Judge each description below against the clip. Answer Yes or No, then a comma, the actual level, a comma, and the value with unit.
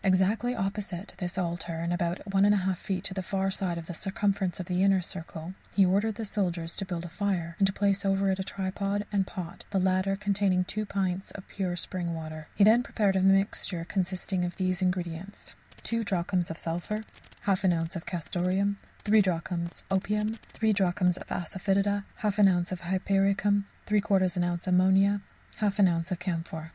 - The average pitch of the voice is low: No, high, 190 Hz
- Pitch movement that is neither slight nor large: No, narrow, 2.2 semitones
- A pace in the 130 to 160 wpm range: No, average, 185 wpm